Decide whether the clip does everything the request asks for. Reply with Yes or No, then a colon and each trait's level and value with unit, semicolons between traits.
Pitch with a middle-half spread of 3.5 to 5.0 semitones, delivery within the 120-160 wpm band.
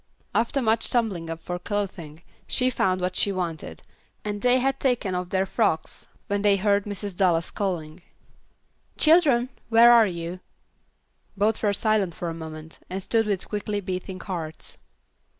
Yes: average, 3.9 semitones; average, 155 wpm